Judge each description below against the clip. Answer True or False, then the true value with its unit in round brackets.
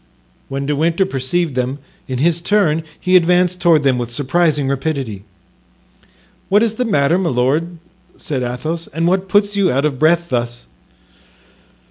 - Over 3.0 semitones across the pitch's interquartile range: True (4.8 semitones)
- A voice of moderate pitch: True (160 Hz)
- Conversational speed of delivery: True (155 wpm)